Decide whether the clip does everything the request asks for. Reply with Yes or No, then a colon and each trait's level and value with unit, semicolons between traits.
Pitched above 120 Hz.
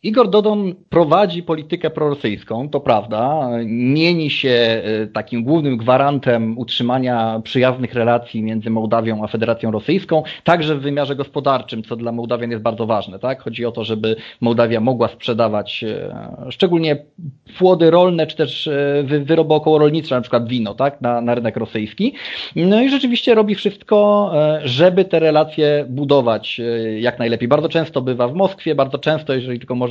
Yes: low, 135 Hz